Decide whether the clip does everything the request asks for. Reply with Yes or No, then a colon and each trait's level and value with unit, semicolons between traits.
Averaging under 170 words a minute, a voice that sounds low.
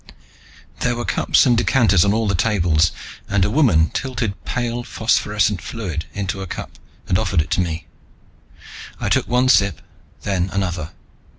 Yes: average, 160 wpm; low, 100 Hz